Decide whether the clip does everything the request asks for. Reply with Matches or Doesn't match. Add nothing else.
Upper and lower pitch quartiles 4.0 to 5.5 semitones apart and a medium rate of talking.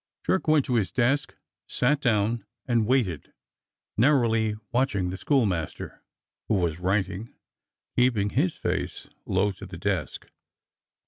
Doesn't match